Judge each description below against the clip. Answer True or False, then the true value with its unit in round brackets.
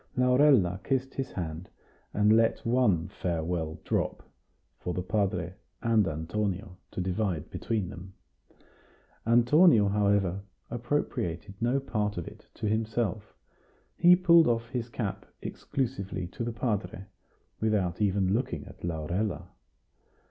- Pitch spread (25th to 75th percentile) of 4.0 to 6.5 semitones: True (4.7 semitones)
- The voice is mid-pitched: False (105 Hz)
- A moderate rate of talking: False (120 wpm)